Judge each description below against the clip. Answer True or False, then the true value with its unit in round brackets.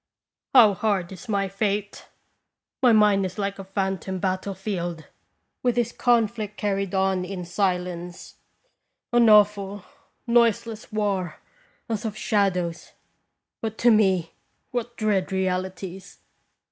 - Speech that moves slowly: True (120 wpm)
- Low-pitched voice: False (200 Hz)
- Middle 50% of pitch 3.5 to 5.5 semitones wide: False (2.4 semitones)